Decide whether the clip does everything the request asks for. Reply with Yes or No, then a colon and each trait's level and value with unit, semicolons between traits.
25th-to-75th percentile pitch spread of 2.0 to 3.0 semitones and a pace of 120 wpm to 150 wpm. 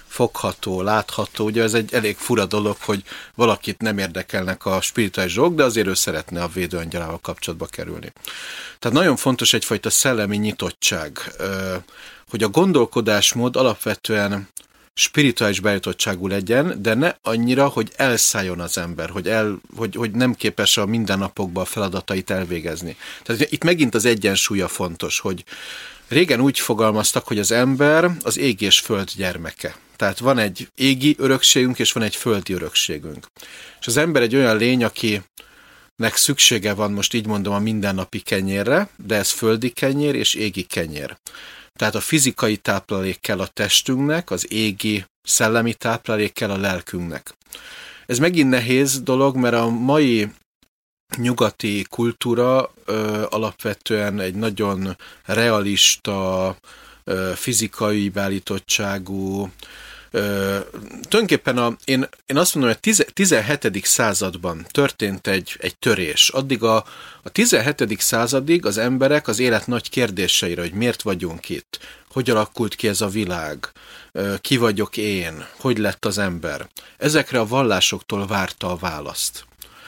No: average, 3.9 semitones; average, 140 wpm